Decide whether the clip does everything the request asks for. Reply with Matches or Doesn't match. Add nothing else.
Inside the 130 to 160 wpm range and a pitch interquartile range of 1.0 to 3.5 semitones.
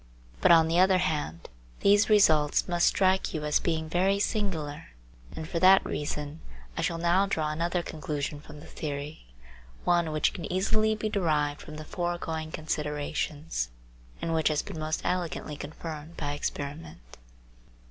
Matches